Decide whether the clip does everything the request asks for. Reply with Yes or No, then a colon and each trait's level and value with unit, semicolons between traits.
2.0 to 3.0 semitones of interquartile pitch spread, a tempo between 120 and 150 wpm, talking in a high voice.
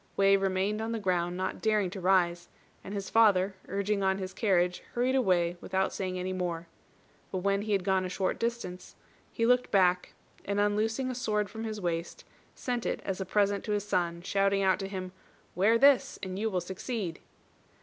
No: narrow, 2.4 semitones; average, 195 wpm; high, 195 Hz